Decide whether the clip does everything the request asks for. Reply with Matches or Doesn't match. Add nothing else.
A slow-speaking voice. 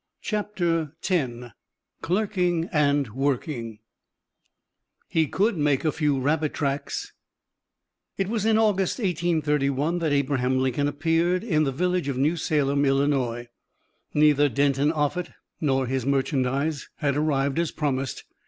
Matches